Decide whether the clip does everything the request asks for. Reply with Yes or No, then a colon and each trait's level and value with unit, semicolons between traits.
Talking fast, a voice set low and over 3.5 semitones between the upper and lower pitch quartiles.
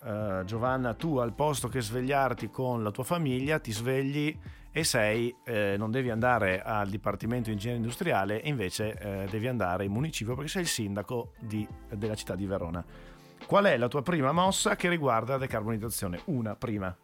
Yes: fast, 180 wpm; low, 115 Hz; average, 4.2 semitones